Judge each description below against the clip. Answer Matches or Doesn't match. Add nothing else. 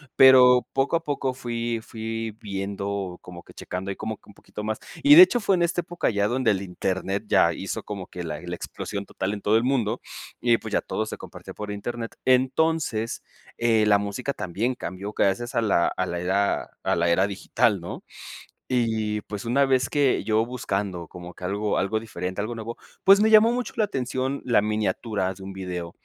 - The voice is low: Matches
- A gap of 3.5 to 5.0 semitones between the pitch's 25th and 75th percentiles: Matches